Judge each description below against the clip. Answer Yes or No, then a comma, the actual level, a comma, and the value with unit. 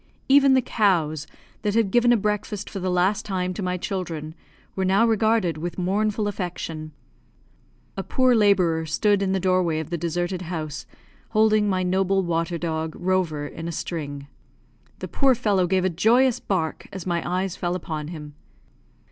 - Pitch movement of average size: Yes, average, 3.7 semitones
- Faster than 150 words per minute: Yes, average, 170 wpm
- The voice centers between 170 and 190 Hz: Yes, medium, 185 Hz